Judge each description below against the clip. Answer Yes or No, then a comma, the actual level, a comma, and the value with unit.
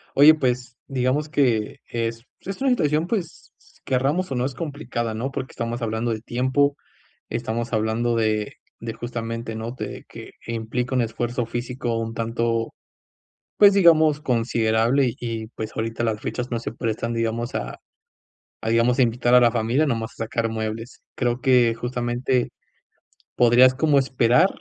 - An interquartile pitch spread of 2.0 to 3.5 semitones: Yes, narrow, 2.4 semitones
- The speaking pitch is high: No, low, 120 Hz